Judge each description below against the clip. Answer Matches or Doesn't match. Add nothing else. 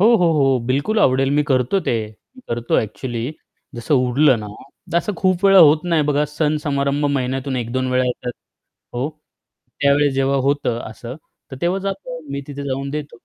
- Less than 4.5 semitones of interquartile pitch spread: Matches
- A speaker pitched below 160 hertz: Matches